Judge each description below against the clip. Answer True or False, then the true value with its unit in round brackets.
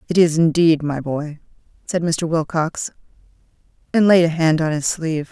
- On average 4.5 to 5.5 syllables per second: True (4.9 syllables/s)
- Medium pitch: True (160 Hz)